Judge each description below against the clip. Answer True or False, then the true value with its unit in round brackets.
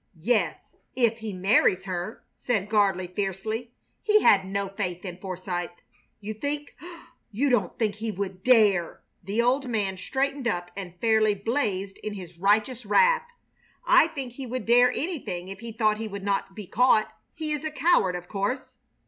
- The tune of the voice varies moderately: True (4.5 semitones)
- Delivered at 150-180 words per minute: True (170 wpm)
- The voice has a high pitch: True (215 Hz)